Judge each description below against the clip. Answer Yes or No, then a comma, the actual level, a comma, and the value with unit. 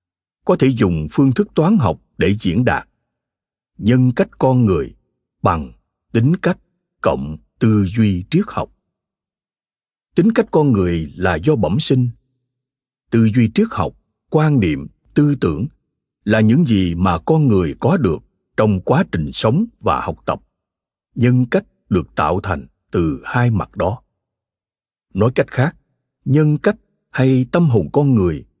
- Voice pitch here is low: Yes, low, 120 Hz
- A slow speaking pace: Yes, slow, 150 wpm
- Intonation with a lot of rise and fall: Yes, wide, 7.3 semitones